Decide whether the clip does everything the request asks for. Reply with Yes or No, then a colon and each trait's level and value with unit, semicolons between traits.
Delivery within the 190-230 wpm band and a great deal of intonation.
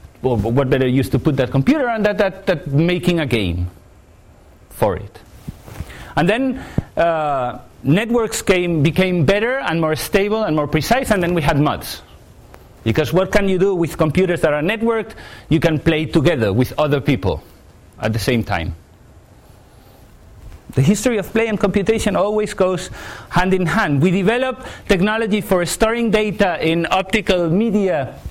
No: average, 160 wpm; wide, 6.7 semitones